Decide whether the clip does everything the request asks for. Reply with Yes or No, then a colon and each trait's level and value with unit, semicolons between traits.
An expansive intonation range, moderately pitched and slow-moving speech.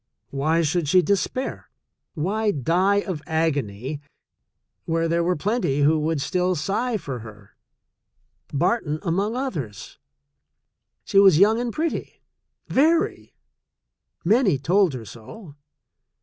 Yes: wide, 5.8 semitones; medium, 170 Hz; slow, 120 wpm